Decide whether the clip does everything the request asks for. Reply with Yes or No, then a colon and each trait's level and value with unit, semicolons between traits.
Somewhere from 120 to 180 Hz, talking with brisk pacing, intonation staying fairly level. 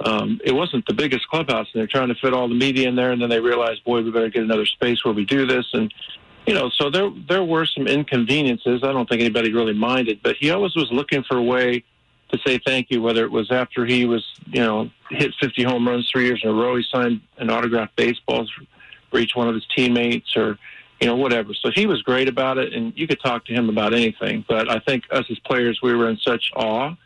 Yes: low, 125 Hz; fast, 255 wpm; narrow, 2.1 semitones